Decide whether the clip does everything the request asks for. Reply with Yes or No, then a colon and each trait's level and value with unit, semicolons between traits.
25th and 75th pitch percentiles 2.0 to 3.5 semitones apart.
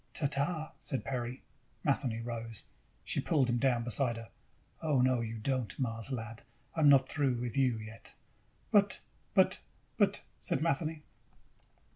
Yes: average, 3.2 semitones